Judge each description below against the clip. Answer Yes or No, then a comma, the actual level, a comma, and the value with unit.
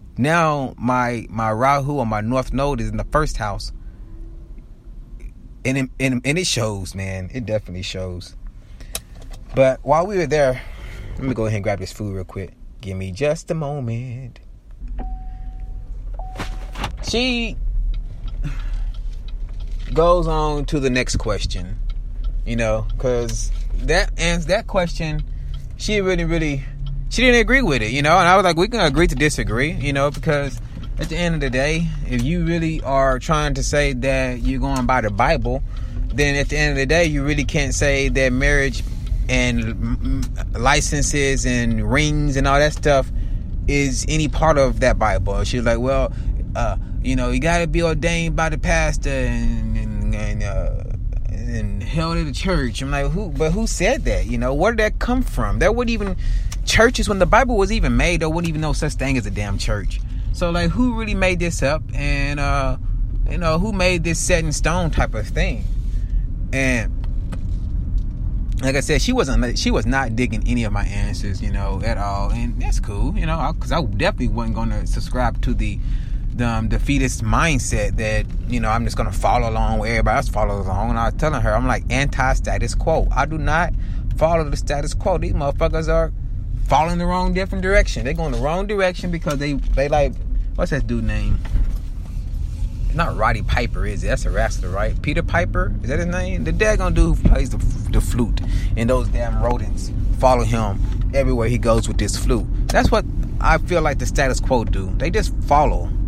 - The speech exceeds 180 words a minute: Yes, average, 190 wpm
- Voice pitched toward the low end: Yes, low, 120 Hz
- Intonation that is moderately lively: No, wide, 5.7 semitones